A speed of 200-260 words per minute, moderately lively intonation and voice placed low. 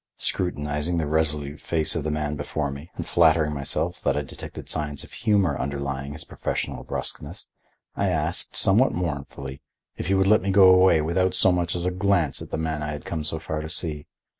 Yes: fast, 205 wpm; average, 3.4 semitones; very low, 80 Hz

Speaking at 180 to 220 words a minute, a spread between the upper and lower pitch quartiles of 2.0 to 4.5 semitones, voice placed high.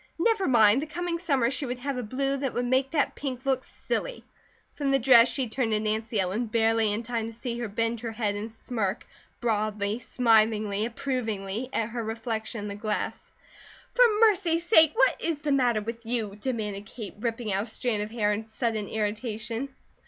Yes: average, 190 wpm; average, 3.4 semitones; high, 230 Hz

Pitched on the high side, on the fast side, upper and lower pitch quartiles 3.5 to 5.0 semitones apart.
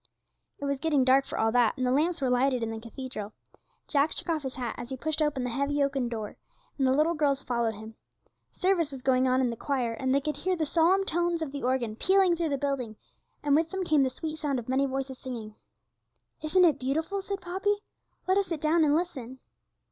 Yes: very high, 275 Hz; fast, 230 wpm; average, 4.1 semitones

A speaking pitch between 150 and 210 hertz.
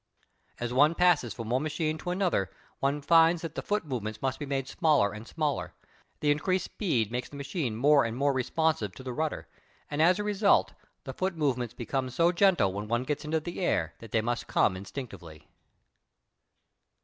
No: medium, 140 Hz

